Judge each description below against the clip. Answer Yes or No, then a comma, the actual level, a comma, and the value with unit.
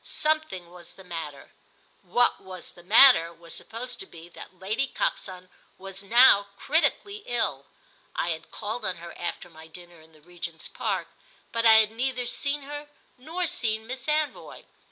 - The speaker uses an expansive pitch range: Yes, wide, 6.6 semitones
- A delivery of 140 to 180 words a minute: Yes, average, 165 wpm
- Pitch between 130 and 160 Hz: No, high, 200 Hz